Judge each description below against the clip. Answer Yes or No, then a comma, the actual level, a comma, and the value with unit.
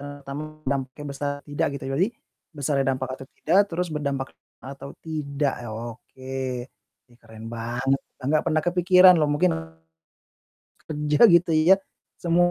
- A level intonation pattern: No, average, 3.1 semitones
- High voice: No, medium, 145 Hz